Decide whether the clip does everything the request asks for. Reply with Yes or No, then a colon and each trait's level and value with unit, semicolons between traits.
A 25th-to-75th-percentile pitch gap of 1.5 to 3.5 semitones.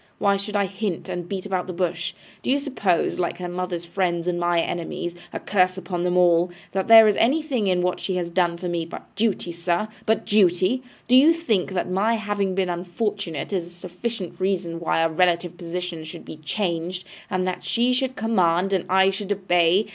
Yes: average, 2.8 semitones